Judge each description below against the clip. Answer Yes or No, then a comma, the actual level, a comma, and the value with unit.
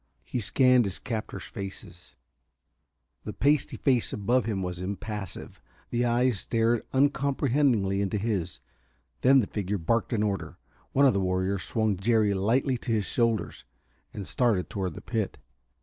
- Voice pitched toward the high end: No, low, 110 Hz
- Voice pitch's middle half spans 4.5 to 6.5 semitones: No, average, 4.0 semitones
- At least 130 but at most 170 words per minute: Yes, average, 150 wpm